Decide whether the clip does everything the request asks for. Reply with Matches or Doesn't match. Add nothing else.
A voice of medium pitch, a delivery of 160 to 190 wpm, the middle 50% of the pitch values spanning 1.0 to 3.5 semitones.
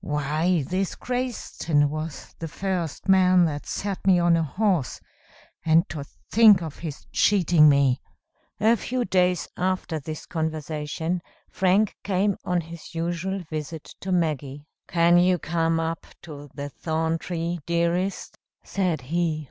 Doesn't match